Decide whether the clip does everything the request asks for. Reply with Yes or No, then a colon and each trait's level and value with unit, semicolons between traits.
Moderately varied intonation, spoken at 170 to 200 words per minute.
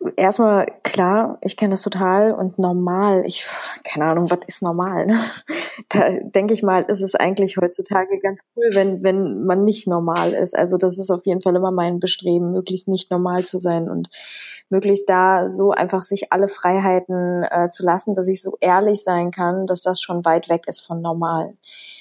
No: narrow, 1.7 semitones; fast, 190 wpm